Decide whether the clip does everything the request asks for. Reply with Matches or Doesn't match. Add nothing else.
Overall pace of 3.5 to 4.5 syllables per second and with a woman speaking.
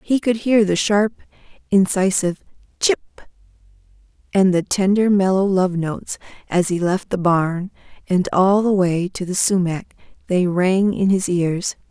Matches